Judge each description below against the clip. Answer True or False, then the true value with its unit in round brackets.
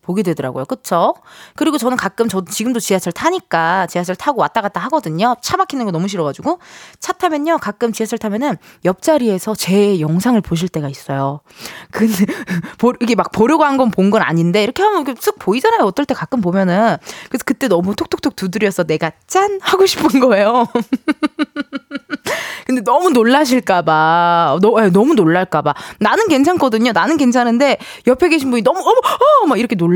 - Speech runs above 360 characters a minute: True (370 characters per minute)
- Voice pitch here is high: True (235 Hz)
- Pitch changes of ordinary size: False (7.6 semitones)